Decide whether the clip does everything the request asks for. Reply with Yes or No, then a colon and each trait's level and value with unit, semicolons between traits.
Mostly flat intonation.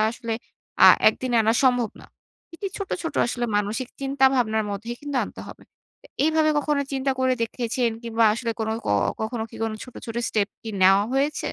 No: average, 3.3 semitones